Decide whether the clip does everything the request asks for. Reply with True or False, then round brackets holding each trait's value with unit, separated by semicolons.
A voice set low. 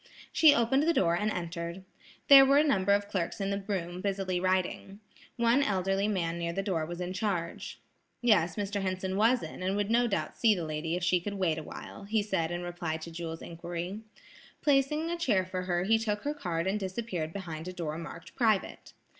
False (190 Hz)